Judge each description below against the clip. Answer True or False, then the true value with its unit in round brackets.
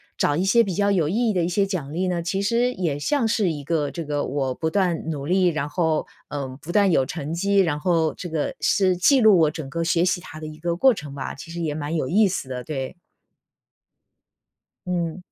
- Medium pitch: True (170 Hz)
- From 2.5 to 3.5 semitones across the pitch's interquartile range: False (4.0 semitones)